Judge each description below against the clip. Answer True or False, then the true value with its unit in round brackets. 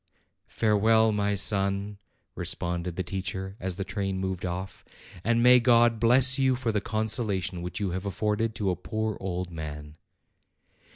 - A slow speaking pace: False (155 wpm)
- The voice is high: False (100 Hz)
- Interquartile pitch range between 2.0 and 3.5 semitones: True (3.1 semitones)